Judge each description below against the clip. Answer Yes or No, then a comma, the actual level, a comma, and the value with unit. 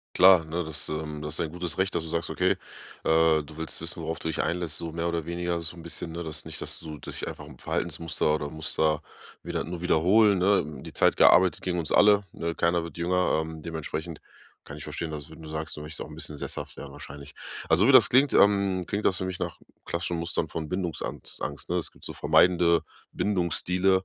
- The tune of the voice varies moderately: No, narrow, 2.2 semitones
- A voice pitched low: Yes, very low, 85 Hz